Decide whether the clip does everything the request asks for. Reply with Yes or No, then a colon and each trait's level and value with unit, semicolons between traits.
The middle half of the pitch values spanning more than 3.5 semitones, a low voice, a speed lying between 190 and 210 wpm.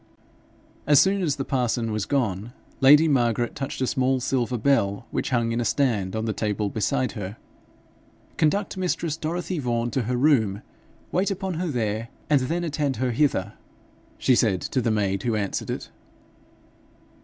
No: average, 4.9 semitones; low, 125 Hz; average, 165 wpm